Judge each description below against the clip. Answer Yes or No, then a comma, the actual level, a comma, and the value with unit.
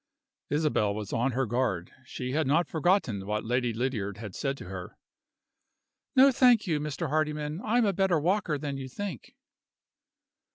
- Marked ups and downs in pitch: Yes, wide, 6.7 semitones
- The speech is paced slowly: No, average, 165 wpm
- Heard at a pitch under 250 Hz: Yes, medium, 140 Hz